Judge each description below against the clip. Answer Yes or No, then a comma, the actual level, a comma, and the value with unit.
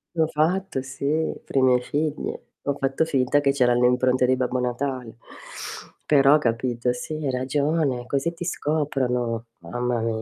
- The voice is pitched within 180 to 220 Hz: No, low, 130 Hz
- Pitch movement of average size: Yes, average, 3.1 semitones